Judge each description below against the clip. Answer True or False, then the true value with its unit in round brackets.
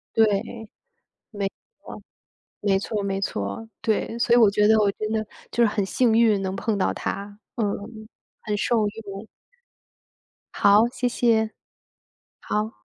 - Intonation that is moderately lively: False (2.0 semitones)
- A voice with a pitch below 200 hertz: False (215 Hz)